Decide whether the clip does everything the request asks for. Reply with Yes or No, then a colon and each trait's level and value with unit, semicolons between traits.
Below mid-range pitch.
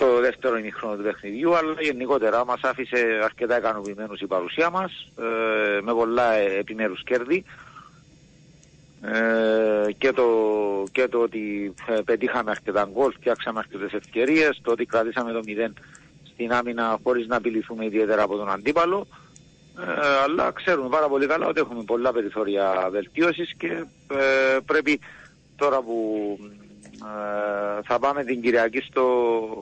Yes: low, 115 Hz